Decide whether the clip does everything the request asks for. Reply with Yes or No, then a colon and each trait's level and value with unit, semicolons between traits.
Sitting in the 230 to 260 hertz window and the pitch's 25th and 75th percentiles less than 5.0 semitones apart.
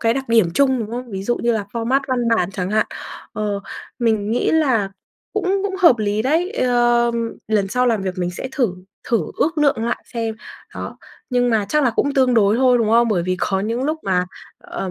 Yes: high, 235 Hz; average, 3.8 semitones